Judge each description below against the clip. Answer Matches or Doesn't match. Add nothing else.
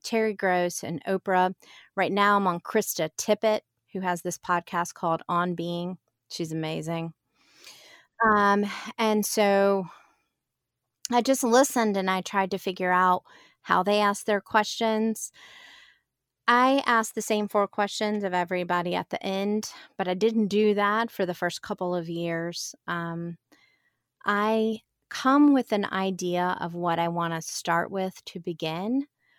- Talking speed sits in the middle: Matches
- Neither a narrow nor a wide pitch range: Matches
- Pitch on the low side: Doesn't match